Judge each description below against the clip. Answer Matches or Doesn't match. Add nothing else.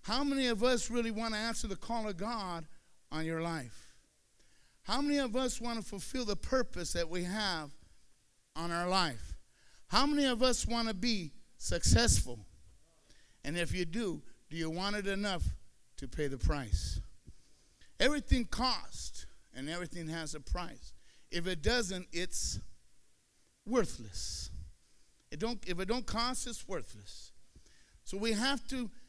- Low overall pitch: Doesn't match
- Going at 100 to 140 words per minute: Doesn't match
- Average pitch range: Doesn't match